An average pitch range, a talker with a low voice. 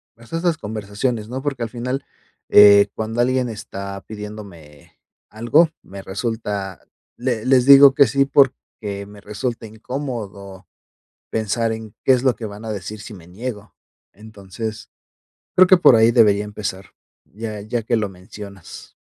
Yes: average, 3.3 semitones; low, 110 Hz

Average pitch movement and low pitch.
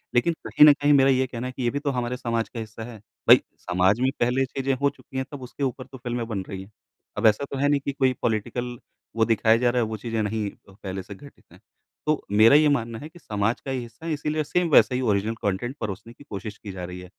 Yes: average, 3.9 semitones; low, 120 Hz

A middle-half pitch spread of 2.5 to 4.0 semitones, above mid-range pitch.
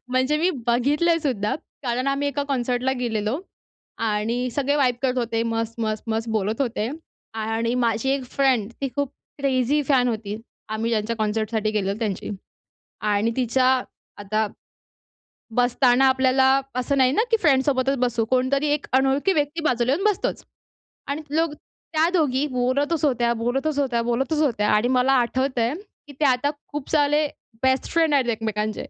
Yes: average, 3.5 semitones; very high, 255 Hz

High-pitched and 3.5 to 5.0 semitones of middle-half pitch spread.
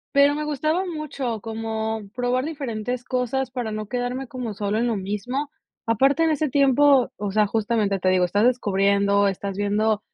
Yes: high, 235 Hz; average, 4.5 semitones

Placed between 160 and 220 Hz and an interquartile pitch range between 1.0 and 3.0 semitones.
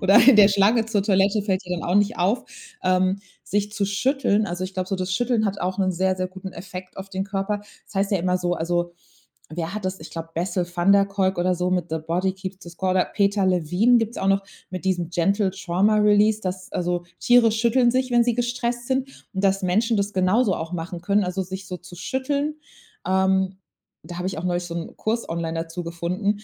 Yes: high, 190 Hz; narrow, 2.6 semitones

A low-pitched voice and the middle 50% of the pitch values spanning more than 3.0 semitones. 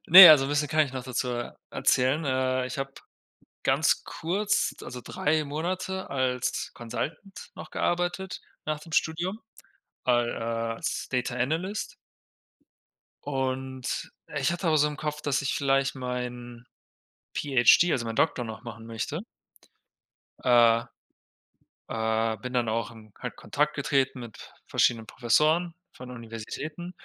Yes: low, 130 Hz; average, 4.3 semitones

